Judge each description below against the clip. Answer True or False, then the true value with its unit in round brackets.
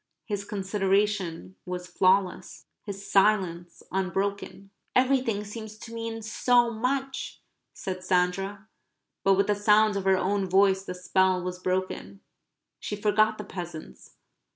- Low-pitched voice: False (195 Hz)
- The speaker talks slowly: True (130 wpm)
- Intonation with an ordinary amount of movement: False (2.3 semitones)